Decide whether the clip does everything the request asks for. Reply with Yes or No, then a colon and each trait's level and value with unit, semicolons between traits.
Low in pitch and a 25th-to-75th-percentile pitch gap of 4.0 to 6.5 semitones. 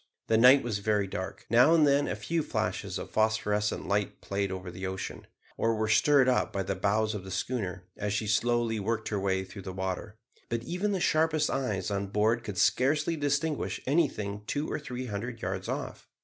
Yes: low, 110 Hz; average, 4.7 semitones